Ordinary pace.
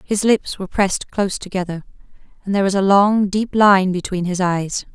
Yes: average, 195 wpm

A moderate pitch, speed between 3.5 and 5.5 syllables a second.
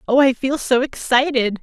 No: very high, 260 Hz; 4.8 syllables/s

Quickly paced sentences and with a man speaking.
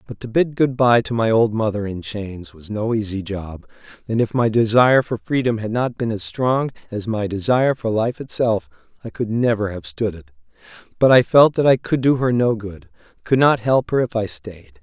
Yes: fast, 225 wpm; male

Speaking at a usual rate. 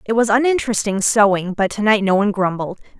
Yes: average, 180 wpm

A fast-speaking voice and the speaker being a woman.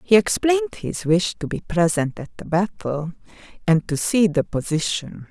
No: average, 170 wpm; female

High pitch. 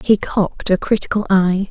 Yes: high, 195 Hz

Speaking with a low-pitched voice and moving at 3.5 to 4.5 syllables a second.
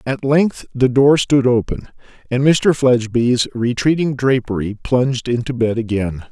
Yes: low, 125 Hz; 4.4 syllables/s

